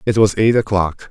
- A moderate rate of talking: No, fast, 215 wpm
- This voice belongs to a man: Yes, male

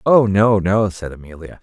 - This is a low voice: Yes, low, 100 Hz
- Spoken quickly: No, average, 185 wpm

